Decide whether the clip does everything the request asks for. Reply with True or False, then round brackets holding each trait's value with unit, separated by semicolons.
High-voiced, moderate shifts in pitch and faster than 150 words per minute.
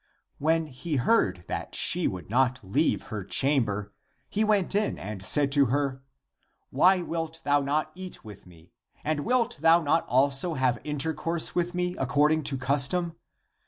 False (145 Hz; 4.4 semitones; 160 wpm)